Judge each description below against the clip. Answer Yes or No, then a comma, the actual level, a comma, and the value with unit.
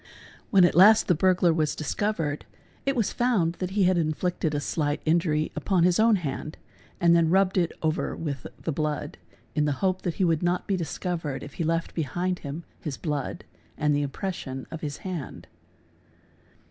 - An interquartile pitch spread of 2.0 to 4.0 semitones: Yes, average, 3.3 semitones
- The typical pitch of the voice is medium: Yes, medium, 165 Hz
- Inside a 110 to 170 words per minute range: No, average, 185 wpm